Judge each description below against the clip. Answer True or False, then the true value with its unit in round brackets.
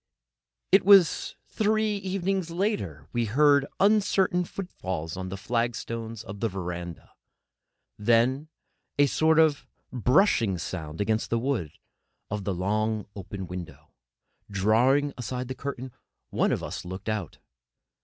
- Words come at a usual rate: False (130 wpm)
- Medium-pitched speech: False (115 Hz)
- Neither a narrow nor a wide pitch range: False (8.2 semitones)